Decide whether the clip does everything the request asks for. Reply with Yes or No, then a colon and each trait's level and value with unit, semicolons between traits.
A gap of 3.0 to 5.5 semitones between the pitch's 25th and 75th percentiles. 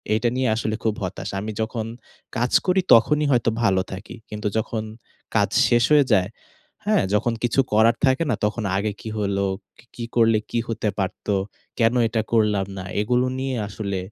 No: narrow, 2.6 semitones